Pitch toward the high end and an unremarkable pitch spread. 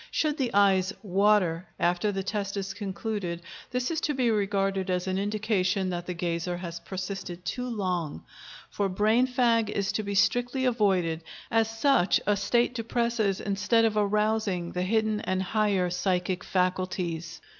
Yes: high, 200 Hz; average, 3.3 semitones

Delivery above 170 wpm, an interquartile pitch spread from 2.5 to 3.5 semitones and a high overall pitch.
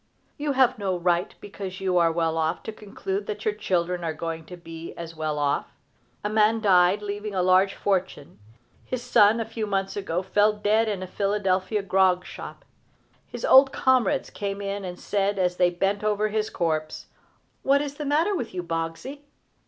Yes: average, 185 wpm; average, 3.1 semitones; high, 195 Hz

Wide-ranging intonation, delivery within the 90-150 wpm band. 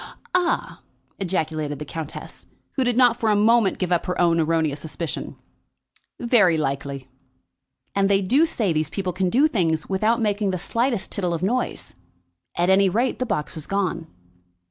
No: wide, 5.7 semitones; average, 165 wpm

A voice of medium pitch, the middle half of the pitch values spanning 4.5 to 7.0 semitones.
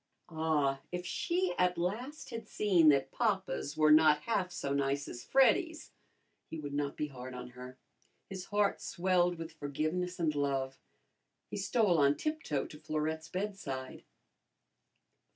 Yes: medium, 160 Hz; average, 5.2 semitones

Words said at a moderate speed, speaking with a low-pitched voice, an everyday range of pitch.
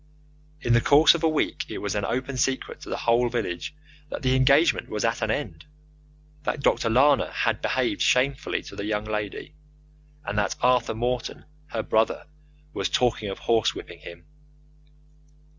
Yes: average, 170 wpm; low, 120 Hz; average, 3.6 semitones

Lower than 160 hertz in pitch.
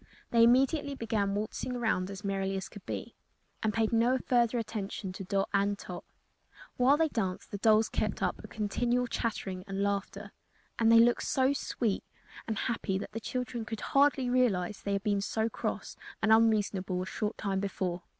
No: high, 220 Hz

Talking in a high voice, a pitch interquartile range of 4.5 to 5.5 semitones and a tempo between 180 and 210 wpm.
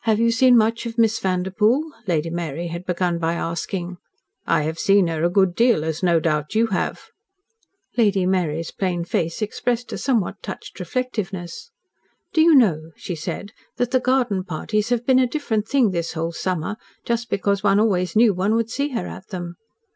Yes: high, 195 Hz; average, 5.1 semitones; average, 185 wpm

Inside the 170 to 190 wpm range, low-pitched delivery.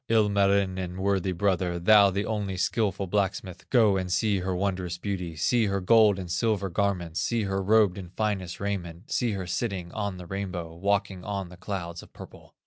Yes: average, 180 wpm; very low, 95 Hz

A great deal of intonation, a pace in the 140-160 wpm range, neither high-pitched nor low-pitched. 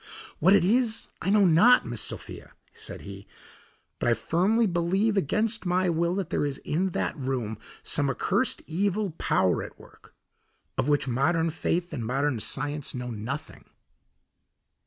Yes: wide, 6.3 semitones; average, 155 wpm; medium, 165 Hz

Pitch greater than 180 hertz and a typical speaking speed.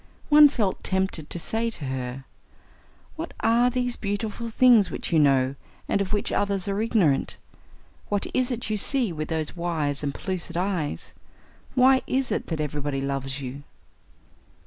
Yes: high, 190 Hz; average, 160 wpm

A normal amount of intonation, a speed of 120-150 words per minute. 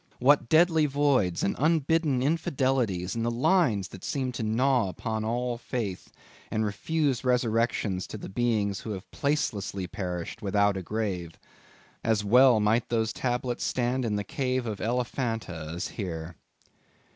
Yes: average, 4.2 semitones; average, 145 wpm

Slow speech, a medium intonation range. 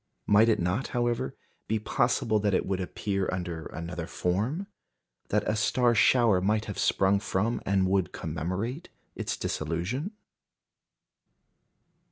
Yes: slow, 130 wpm; average, 4.0 semitones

